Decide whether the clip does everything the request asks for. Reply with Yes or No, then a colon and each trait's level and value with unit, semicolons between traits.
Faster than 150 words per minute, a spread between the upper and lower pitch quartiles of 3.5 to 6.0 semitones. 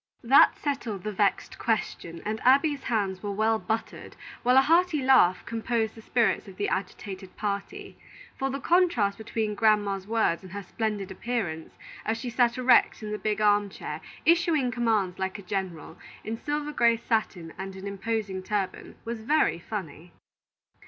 Yes: average, 165 wpm; average, 3.8 semitones